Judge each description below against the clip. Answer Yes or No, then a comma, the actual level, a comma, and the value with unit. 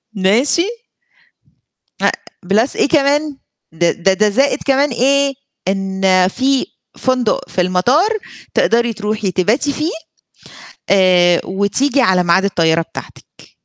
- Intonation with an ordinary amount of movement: No, wide, 6.5 semitones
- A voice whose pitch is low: No, high, 215 Hz